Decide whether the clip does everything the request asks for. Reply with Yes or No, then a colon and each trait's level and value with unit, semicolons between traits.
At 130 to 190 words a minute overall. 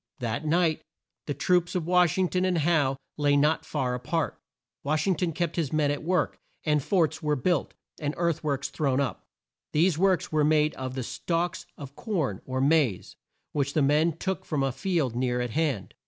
No: average, 200 wpm